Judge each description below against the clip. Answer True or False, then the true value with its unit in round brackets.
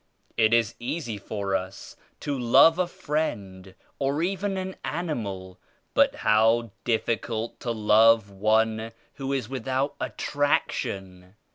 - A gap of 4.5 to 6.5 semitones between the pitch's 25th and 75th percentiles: True (5.2 semitones)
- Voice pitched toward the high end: False (115 Hz)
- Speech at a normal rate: False (120 wpm)